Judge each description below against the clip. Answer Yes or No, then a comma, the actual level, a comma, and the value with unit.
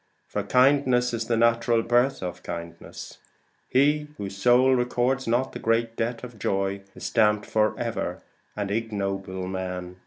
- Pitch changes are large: No, average, 4.0 semitones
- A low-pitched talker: Yes, low, 115 Hz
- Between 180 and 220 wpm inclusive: No, average, 145 wpm